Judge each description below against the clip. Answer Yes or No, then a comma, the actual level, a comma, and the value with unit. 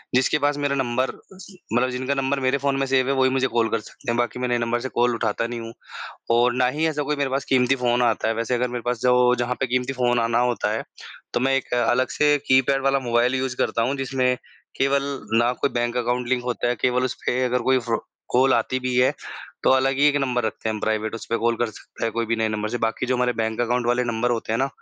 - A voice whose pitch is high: No, low, 125 Hz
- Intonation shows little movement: Yes, narrow, 1.9 semitones